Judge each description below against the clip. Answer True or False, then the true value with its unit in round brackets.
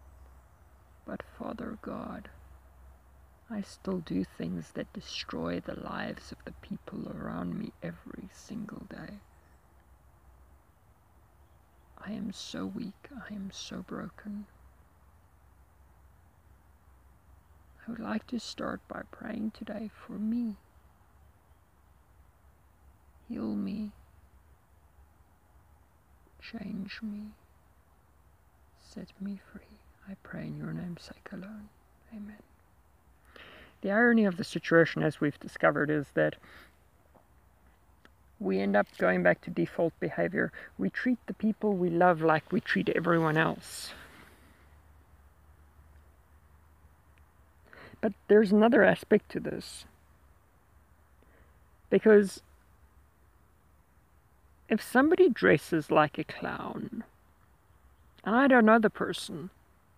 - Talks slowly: True (100 wpm)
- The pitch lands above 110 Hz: False (85 Hz)